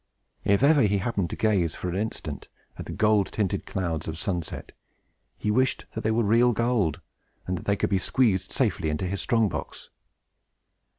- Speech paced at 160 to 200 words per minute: Yes, average, 185 wpm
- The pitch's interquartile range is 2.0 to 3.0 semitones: No, average, 3.7 semitones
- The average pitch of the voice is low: Yes, low, 100 Hz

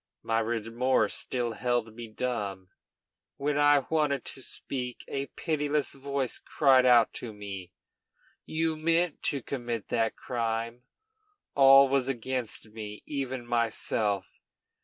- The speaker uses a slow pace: Yes, slow, 120 wpm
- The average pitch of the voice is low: Yes, low, 125 Hz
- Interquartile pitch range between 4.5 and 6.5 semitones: No, average, 3.5 semitones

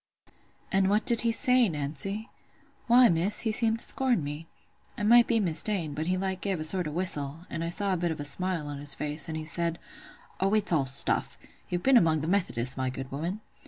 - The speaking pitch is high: No, medium, 175 Hz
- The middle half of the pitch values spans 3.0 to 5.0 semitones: No, wide, 5.5 semitones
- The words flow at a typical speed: No, fast, 225 wpm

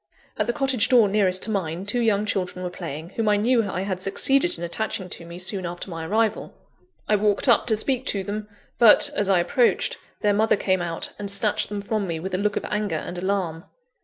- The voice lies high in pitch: Yes, high, 200 Hz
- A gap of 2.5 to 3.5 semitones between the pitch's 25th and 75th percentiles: Yes, average, 2.9 semitones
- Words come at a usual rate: No, fast, 225 wpm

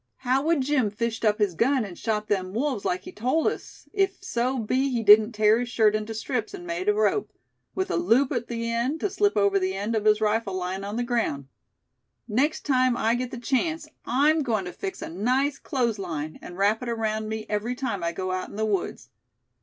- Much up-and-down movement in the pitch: No, average, 4.3 semitones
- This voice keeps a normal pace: No, fast, 225 wpm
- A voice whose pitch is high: Yes, high, 230 Hz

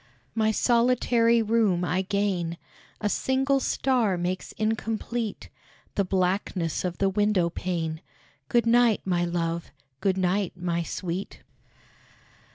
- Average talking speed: No, slow, 115 wpm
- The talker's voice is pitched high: Yes, high, 195 Hz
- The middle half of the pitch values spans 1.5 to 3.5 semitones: No, average, 4.3 semitones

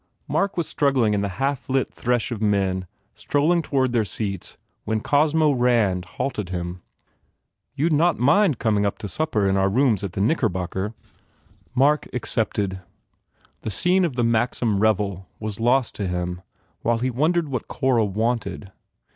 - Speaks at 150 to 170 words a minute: Yes, average, 160 wpm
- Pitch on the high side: No, low, 115 Hz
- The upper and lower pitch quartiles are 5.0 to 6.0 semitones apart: Yes, wide, 5.5 semitones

